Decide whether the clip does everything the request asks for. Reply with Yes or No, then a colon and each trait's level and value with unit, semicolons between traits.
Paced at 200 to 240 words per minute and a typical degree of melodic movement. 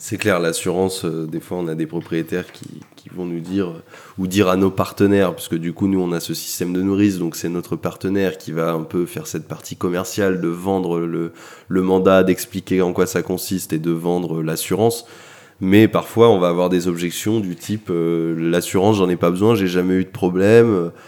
No: average, 215 wpm; narrow, 2.3 semitones